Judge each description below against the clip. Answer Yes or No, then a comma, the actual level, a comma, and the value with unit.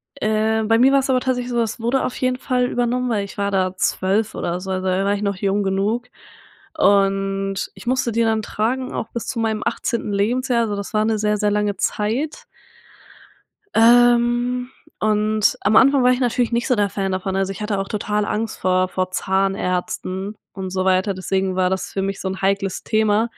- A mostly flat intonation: No, average, 3.4 semitones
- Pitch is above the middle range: Yes, high, 210 Hz